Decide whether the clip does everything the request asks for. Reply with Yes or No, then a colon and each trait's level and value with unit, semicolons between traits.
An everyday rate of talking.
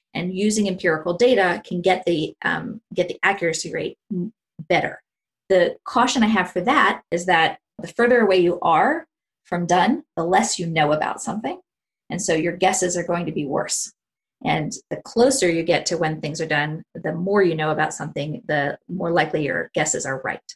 Yes: average, 195 wpm